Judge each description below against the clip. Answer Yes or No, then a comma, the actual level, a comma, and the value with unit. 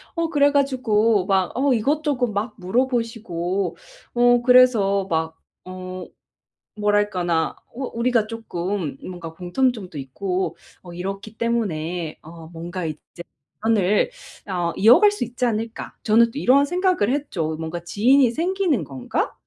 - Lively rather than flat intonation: Yes, wide, 5.9 semitones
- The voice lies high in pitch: Yes, high, 210 Hz